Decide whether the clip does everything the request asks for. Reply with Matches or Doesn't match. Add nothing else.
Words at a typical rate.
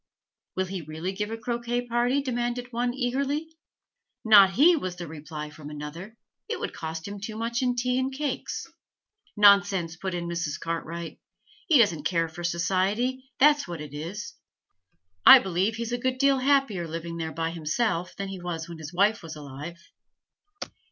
Matches